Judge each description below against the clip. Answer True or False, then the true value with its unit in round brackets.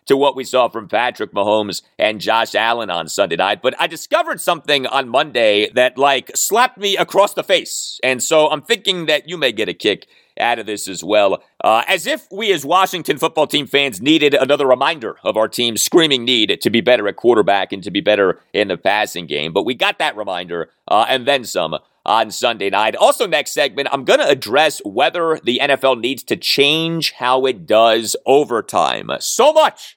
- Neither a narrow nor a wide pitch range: False (6.3 semitones)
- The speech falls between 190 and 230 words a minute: True (205 wpm)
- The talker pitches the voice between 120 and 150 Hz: True (140 Hz)